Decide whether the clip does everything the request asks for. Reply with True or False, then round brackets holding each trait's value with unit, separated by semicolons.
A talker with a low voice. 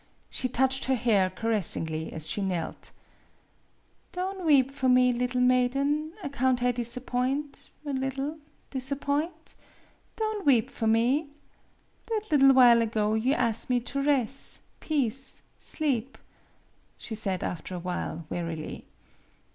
False (255 Hz)